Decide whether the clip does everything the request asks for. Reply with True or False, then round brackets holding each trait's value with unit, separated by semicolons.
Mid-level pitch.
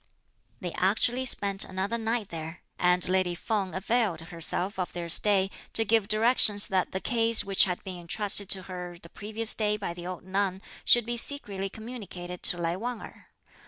False (195 Hz)